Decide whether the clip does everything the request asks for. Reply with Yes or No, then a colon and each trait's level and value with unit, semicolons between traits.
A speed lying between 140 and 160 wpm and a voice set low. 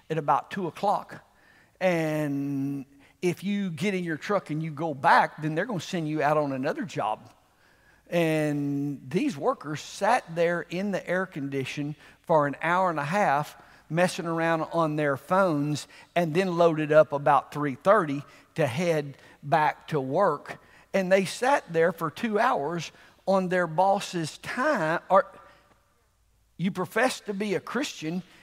No: average, 155 wpm; medium, 165 Hz